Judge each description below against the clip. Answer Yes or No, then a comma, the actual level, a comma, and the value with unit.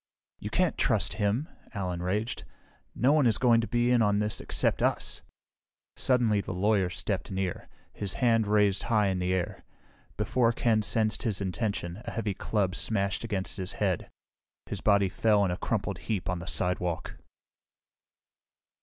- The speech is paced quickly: No, average, 165 wpm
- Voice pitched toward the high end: No, low, 105 Hz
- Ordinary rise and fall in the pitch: Yes, average, 3.3 semitones